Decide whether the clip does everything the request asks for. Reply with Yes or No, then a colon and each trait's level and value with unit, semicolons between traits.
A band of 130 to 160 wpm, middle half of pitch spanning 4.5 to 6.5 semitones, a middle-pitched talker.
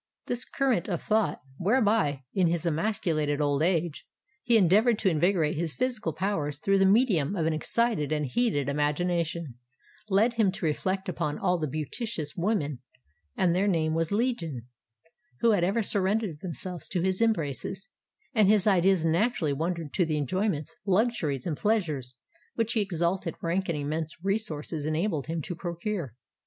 Yes: average, 155 wpm; average, 5.1 semitones; medium, 175 Hz